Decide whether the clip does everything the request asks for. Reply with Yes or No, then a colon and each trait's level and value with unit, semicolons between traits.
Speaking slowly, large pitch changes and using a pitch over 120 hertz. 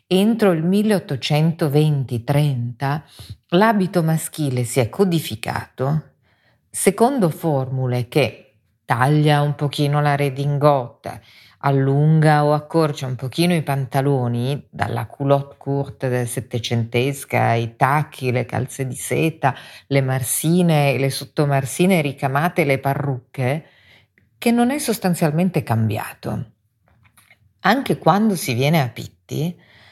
No: slow, 105 wpm; average, 4.3 semitones; medium, 140 Hz